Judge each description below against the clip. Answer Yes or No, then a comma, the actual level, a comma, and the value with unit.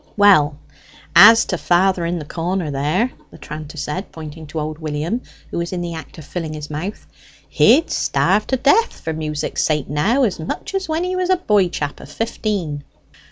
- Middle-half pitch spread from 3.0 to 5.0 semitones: No, wide, 5.6 semitones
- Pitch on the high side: No, medium, 170 Hz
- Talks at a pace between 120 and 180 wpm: No, average, 195 wpm